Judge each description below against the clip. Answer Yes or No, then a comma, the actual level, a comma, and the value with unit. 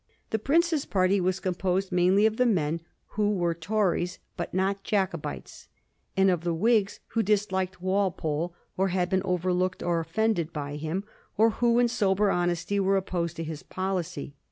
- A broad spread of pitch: No, narrow, 2.6 semitones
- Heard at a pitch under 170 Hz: No, medium, 185 Hz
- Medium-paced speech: Yes, average, 170 wpm